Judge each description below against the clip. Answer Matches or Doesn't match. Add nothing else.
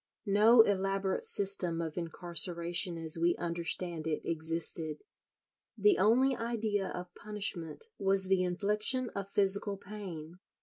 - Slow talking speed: Matches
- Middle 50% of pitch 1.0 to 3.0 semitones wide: Doesn't match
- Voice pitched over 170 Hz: Matches